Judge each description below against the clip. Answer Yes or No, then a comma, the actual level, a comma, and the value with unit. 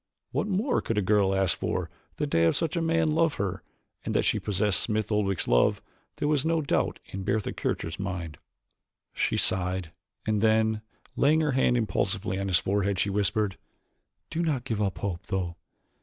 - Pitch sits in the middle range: No, low, 105 Hz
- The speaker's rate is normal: Yes, average, 185 wpm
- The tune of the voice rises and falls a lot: Yes, wide, 6.3 semitones